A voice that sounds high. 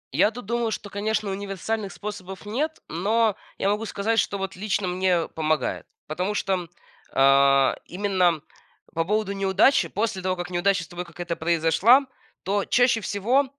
Yes: high, 195 Hz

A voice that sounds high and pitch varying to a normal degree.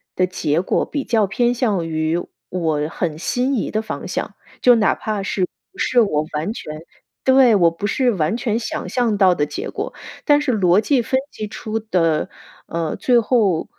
No: high, 205 Hz; wide, 6.2 semitones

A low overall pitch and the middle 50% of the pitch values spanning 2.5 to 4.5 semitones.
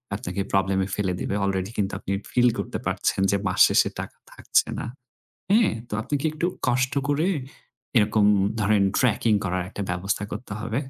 Yes: low, 105 Hz; average, 4.0 semitones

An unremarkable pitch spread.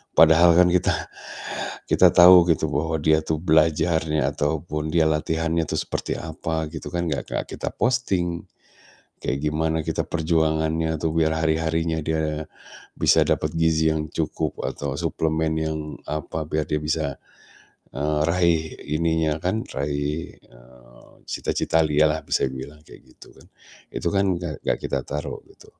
No: narrow, 1.2 semitones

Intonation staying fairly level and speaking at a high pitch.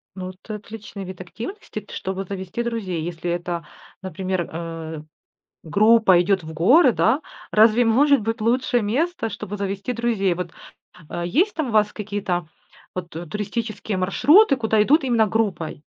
No: average, 4.2 semitones; high, 205 Hz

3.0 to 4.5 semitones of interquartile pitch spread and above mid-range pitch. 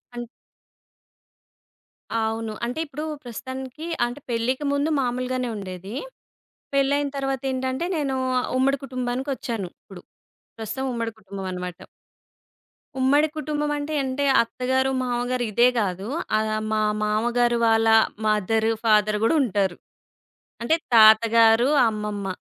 Yes: average, 3.4 semitones; high, 240 Hz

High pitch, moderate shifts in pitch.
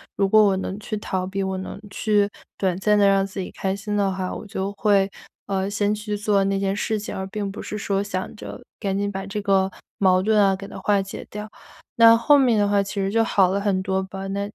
No: high, 200 Hz; narrow, 1.3 semitones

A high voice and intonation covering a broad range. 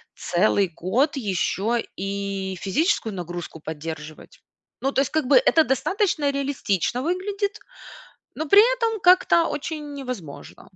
Yes: very high, 255 Hz; wide, 9.0 semitones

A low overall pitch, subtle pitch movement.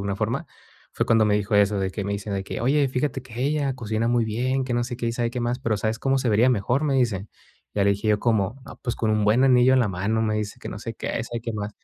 No: low, 115 Hz; average, 3.3 semitones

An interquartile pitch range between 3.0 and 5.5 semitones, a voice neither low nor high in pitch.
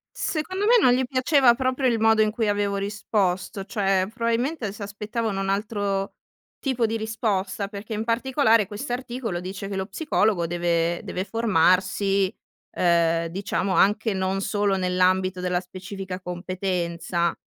No: average, 3.4 semitones; high, 200 Hz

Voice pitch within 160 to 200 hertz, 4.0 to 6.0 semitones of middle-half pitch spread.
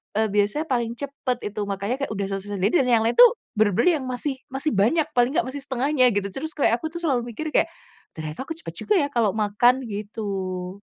No: high, 240 Hz; average, 5.2 semitones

